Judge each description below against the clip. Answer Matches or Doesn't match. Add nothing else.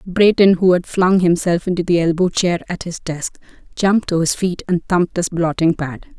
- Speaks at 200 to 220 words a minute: Matches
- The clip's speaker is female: Matches